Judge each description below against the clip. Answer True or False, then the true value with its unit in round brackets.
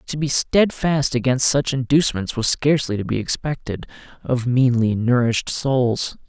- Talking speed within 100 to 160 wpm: True (145 wpm)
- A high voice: False (130 Hz)